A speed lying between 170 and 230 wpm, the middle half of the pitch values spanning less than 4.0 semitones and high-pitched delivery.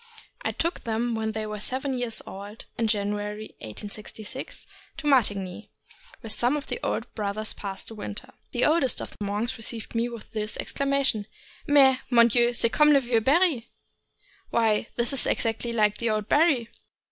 Yes: average, 175 wpm; average, 3.5 semitones; high, 230 Hz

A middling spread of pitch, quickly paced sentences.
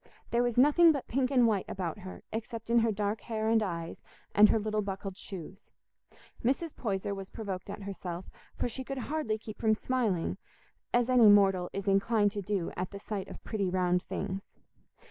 No: average, 3.3 semitones; average, 190 wpm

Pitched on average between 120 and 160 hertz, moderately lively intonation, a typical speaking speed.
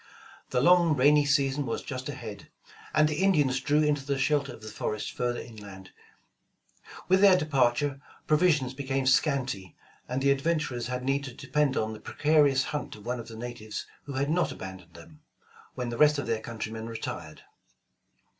Yes: low, 135 Hz; average, 4.1 semitones; average, 175 wpm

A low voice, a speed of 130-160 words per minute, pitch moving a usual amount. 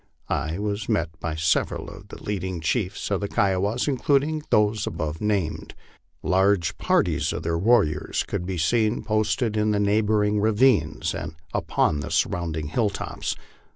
Yes: low, 100 Hz; average, 150 wpm; average, 4.4 semitones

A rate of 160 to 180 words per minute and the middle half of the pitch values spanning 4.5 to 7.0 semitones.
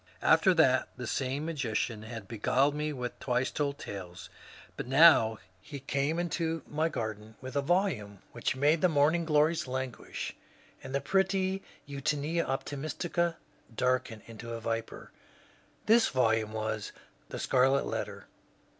No: average, 145 wpm; wide, 5.4 semitones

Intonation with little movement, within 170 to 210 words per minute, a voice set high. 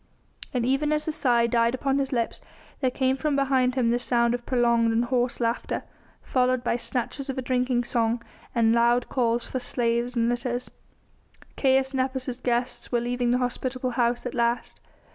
Yes: narrow, 1.5 semitones; average, 180 wpm; high, 245 Hz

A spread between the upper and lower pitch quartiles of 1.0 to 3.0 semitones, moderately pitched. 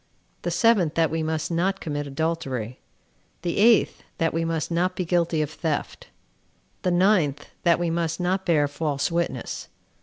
Yes: narrow, 2.4 semitones; medium, 165 Hz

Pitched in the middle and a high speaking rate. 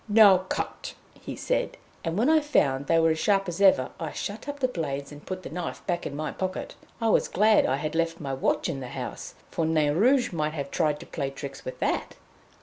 Yes: medium, 165 Hz; fast, 235 wpm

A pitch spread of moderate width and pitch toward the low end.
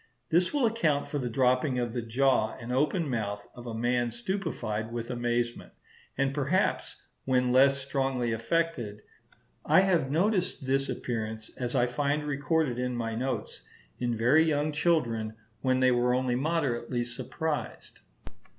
Yes: average, 3.8 semitones; low, 130 Hz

